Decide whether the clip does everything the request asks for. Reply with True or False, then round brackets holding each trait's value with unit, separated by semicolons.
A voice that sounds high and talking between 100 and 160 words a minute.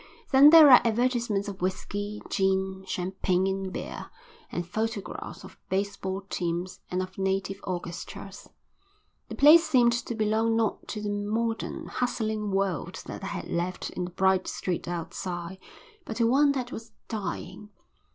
True (200 Hz; 150 wpm)